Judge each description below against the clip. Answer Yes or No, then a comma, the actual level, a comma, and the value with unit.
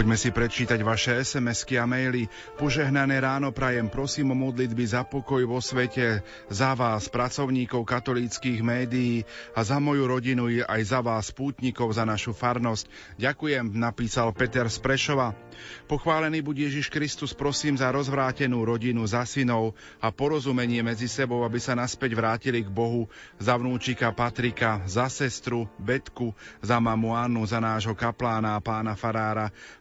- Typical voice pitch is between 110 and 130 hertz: Yes, low, 120 Hz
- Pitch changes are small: Yes, narrow, 2.3 semitones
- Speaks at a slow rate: No, average, 145 wpm